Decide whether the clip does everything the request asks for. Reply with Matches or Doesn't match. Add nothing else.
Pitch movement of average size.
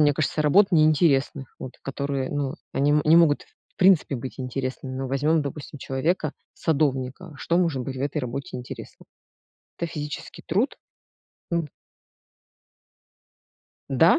Matches